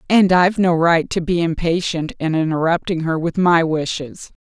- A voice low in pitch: No, medium, 165 Hz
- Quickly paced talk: No, average, 175 wpm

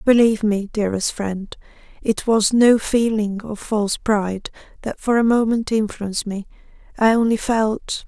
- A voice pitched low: No, high, 215 Hz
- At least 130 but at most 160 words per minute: Yes, average, 150 wpm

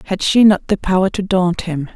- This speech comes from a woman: Yes, female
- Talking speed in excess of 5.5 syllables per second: No, 5.2 syllables/s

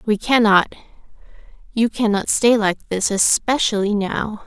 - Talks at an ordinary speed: No, slow, 120 wpm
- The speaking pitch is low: No, high, 215 Hz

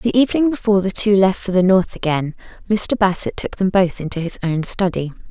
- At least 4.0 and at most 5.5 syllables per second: No, 5.7 syllables/s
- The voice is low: No, high, 190 Hz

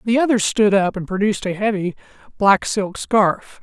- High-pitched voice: Yes, high, 205 Hz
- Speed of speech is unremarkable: Yes, average, 180 wpm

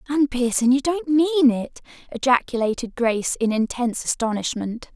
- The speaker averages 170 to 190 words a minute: No, slow, 135 wpm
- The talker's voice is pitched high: Yes, very high, 255 Hz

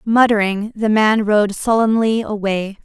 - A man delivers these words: No, female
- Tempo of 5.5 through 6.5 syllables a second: No, 4.1 syllables/s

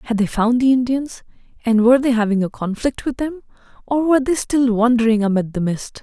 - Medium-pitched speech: No, high, 240 Hz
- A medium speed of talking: No, fast, 210 wpm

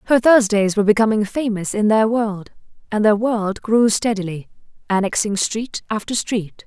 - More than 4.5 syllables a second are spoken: Yes, 4.8 syllables/s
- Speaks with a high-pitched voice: Yes, high, 215 Hz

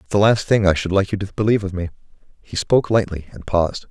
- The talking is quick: Yes, fast, 260 wpm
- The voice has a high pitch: No, low, 100 Hz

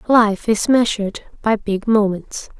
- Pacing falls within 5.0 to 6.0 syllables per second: No, 4.0 syllables/s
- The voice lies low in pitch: No, high, 210 Hz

